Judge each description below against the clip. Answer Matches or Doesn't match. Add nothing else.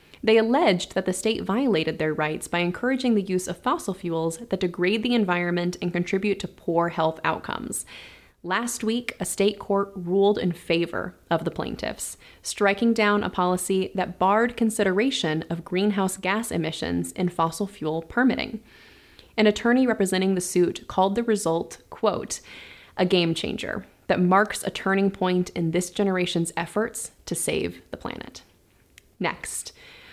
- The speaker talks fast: Doesn't match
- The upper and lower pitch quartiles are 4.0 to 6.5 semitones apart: Doesn't match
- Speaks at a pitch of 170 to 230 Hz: Matches